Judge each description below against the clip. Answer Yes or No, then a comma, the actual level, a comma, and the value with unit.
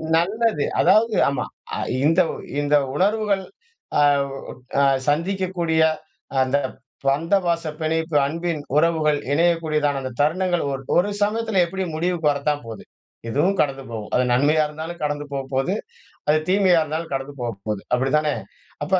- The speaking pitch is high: No, medium, 155 Hz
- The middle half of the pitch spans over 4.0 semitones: No, average, 3.7 semitones